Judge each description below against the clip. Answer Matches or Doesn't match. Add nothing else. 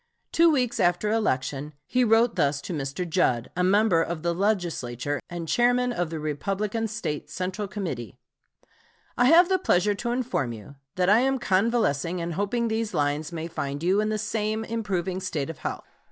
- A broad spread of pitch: Matches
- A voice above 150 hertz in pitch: Matches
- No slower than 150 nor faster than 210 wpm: Matches